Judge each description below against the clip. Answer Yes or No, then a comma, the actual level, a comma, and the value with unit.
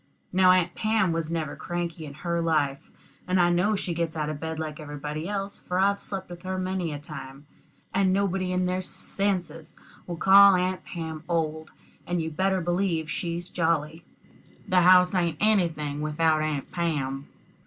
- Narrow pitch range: No, average, 3.0 semitones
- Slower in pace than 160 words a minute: No, average, 175 wpm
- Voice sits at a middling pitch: Yes, medium, 170 Hz